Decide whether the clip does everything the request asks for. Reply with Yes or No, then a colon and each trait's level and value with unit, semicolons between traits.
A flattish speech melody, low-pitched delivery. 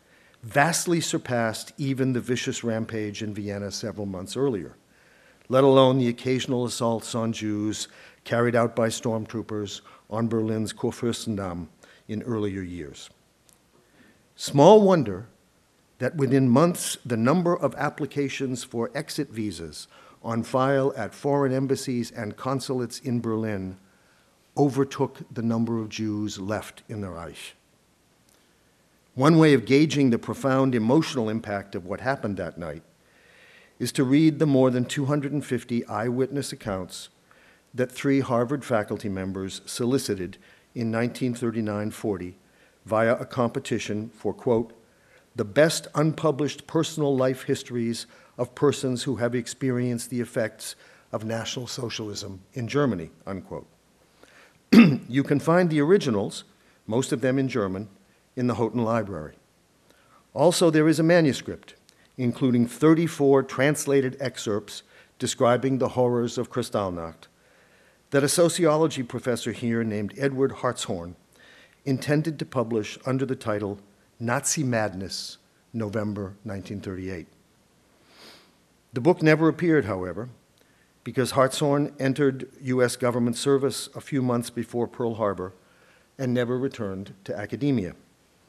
No: average, 4.1 semitones; low, 120 Hz